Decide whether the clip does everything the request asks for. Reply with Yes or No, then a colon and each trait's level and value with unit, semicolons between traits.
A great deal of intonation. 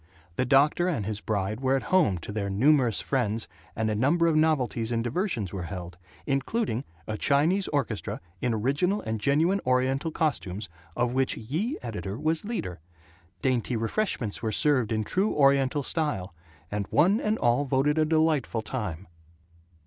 Yes: wide, 6.1 semitones